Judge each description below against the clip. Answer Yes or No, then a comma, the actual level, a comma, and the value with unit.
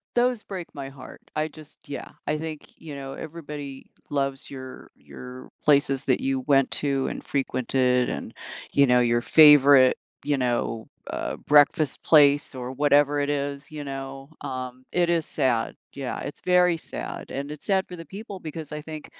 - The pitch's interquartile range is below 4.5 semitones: Yes, narrow, 2.4 semitones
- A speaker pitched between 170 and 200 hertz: No, medium, 140 Hz